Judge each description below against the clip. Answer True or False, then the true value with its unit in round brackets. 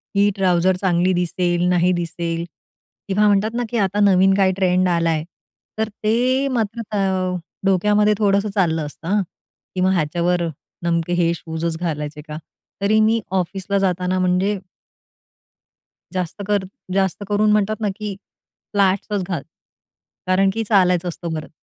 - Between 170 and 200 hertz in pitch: True (185 Hz)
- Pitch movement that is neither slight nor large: True (3.0 semitones)